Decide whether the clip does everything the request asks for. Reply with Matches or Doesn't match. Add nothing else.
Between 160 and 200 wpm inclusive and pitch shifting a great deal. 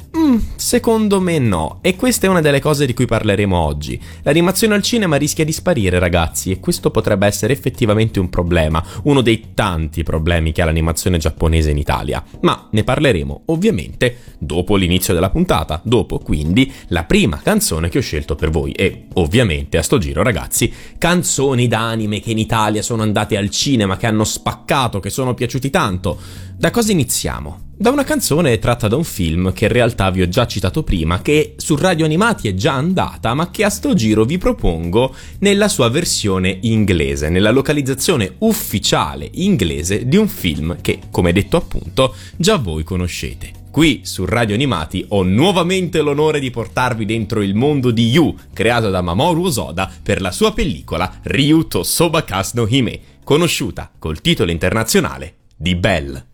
Matches